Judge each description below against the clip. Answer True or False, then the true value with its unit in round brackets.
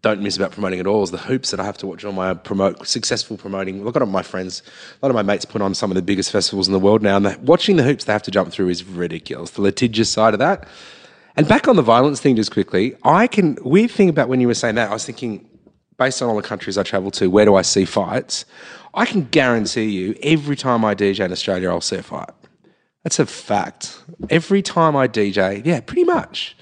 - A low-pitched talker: True (105 Hz)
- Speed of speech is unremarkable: False (255 wpm)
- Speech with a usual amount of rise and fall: False (5.7 semitones)